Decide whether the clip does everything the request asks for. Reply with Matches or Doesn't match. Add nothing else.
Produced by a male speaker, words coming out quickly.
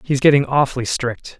Doesn't match